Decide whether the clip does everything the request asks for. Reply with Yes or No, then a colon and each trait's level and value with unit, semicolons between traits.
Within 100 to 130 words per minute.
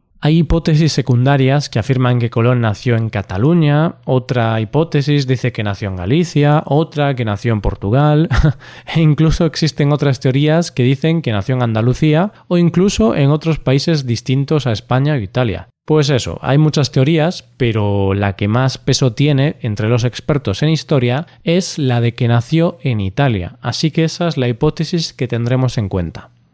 No: average, 175 wpm